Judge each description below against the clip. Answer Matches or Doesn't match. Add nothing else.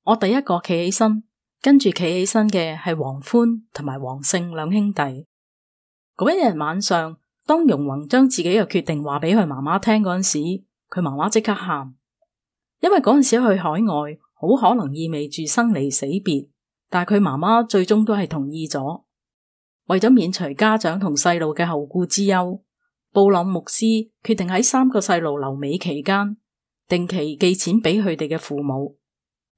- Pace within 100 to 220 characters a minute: Doesn't match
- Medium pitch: Matches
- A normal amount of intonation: Doesn't match